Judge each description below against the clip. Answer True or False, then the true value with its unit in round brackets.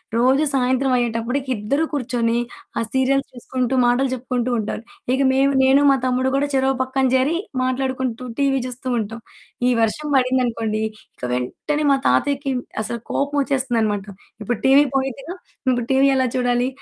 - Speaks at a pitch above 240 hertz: True (260 Hz)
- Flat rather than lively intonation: True (2.0 semitones)